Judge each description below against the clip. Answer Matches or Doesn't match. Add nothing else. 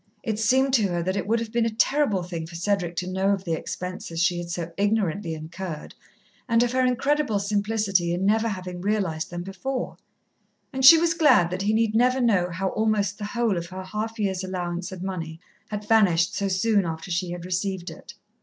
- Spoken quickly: Matches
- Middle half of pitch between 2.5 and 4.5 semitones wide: Matches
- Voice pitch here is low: Doesn't match